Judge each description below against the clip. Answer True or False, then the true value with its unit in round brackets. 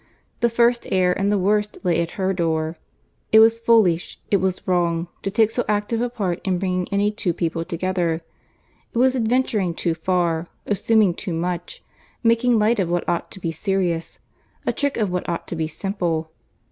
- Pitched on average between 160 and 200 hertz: True (185 Hz)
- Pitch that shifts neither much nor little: True (4.2 semitones)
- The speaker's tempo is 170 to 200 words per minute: True (185 wpm)